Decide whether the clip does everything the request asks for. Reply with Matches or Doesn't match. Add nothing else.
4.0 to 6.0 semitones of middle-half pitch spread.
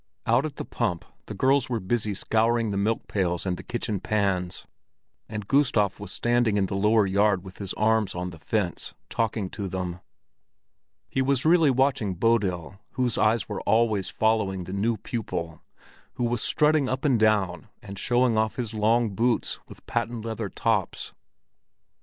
Doesn't match